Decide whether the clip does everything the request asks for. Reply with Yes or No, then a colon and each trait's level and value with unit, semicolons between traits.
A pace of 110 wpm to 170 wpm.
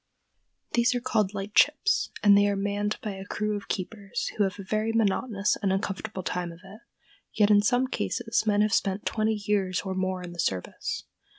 No: average, 195 wpm